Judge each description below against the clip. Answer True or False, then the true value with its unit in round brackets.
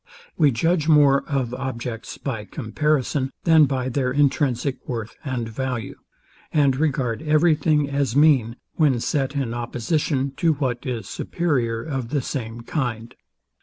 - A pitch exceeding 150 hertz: False (135 Hz)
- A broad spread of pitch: False (3.7 semitones)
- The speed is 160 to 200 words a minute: False (140 wpm)